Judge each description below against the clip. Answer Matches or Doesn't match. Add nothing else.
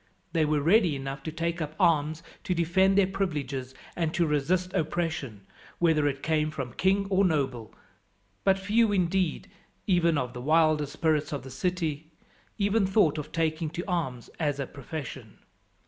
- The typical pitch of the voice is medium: Matches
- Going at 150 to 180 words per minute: Matches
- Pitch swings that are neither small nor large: Matches